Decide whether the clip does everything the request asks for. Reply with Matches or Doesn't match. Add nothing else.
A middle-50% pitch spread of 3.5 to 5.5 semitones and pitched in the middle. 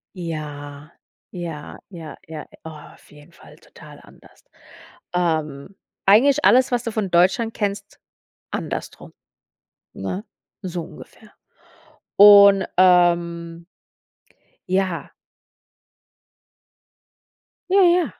Matches